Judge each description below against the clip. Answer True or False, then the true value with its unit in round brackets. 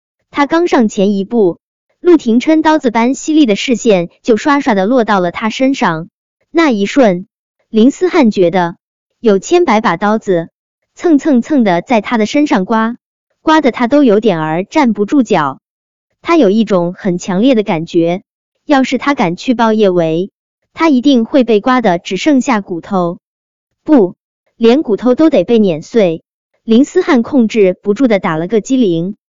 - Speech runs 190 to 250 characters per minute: True (235 characters per minute)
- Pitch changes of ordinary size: False (6.3 semitones)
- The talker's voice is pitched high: True (230 Hz)